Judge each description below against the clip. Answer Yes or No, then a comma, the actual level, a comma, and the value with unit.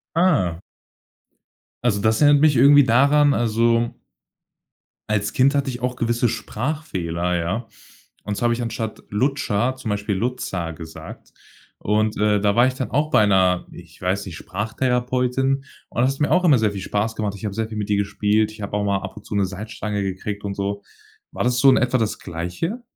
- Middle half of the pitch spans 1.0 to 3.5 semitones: No, average, 4.1 semitones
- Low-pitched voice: Yes, low, 110 Hz